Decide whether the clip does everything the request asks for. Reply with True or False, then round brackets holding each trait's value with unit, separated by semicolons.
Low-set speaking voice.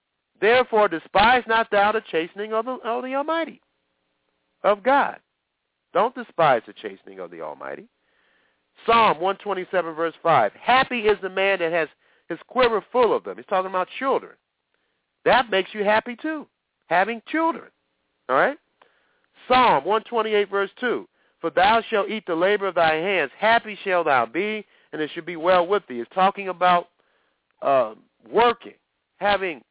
False (205 Hz)